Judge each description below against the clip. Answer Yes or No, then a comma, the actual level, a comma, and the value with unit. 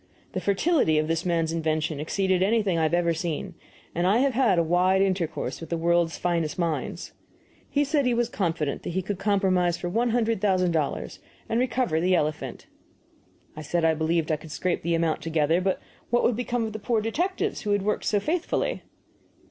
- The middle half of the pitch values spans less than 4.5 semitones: No, average, 5.0 semitones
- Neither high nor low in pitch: Yes, medium, 180 Hz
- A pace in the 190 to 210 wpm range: Yes, average, 195 wpm